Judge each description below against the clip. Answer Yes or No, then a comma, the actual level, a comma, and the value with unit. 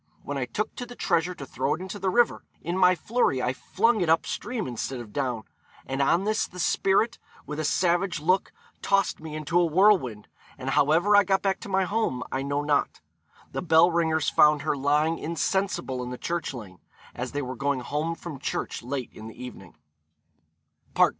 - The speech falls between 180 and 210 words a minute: Yes, average, 195 wpm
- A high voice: No, medium, 160 Hz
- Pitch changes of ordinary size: No, wide, 5.8 semitones